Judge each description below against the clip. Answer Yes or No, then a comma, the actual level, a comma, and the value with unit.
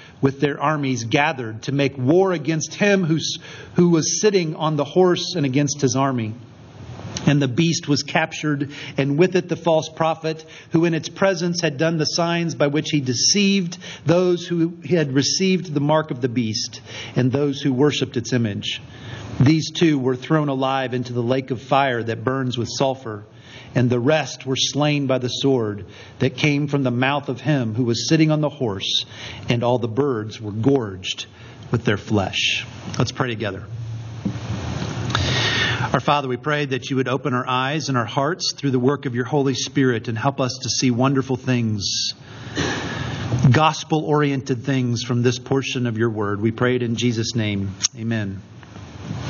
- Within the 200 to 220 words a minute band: No, average, 180 wpm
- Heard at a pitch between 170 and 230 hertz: No, low, 135 Hz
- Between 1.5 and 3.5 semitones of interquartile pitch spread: No, average, 3.9 semitones